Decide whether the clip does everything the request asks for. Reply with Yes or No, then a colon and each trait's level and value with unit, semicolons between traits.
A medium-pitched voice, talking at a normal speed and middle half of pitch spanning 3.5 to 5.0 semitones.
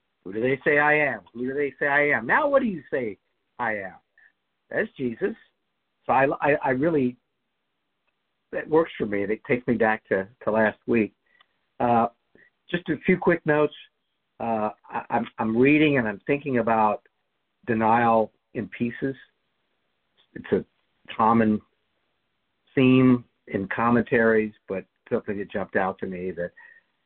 No: low, 125 Hz; average, 155 wpm; average, 4.6 semitones